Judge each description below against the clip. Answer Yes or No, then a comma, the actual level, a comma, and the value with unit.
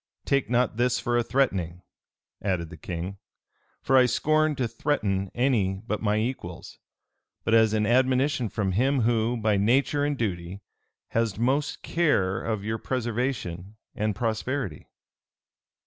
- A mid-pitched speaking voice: No, low, 115 Hz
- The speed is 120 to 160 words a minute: Yes, average, 140 wpm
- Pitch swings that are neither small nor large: Yes, average, 4.7 semitones